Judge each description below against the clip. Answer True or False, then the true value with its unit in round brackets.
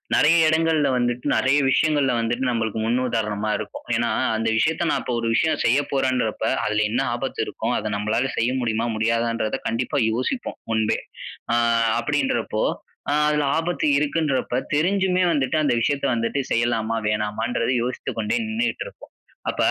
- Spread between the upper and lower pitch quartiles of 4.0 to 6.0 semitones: True (4.5 semitones)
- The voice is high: False (120 Hz)